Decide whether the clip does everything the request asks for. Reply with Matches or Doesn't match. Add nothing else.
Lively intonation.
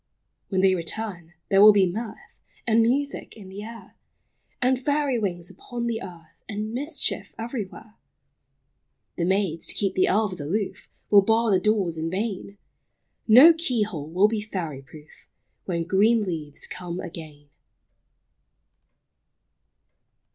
Doesn't match